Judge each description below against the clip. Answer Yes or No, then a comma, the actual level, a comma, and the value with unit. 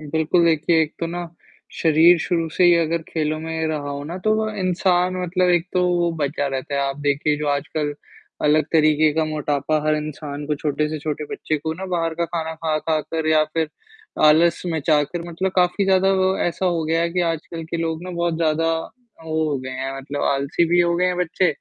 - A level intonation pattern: Yes, narrow, 2.2 semitones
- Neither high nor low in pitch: Yes, medium, 160 Hz